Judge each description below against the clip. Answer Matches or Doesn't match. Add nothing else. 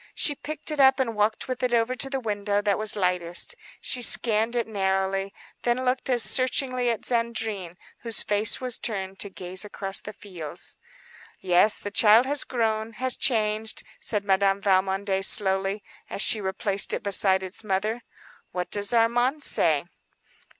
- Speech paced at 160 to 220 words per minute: Matches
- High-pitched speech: Matches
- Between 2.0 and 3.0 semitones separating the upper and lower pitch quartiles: Doesn't match